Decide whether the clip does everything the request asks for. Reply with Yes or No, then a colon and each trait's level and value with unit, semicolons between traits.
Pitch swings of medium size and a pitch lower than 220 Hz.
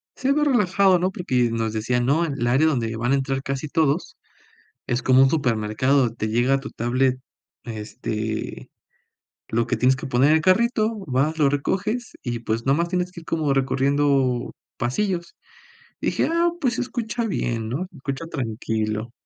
No: wide, 6.1 semitones; low, 135 Hz